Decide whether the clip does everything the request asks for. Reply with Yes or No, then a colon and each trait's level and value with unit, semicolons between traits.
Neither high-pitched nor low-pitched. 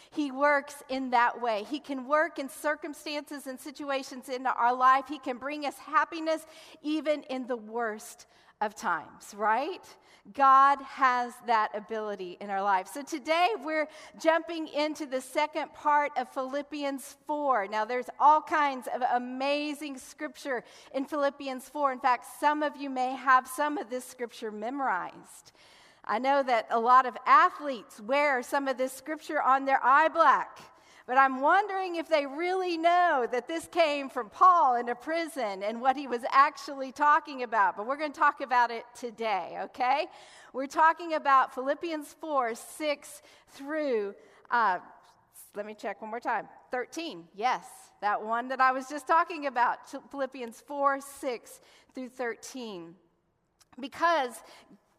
No: very high, 275 Hz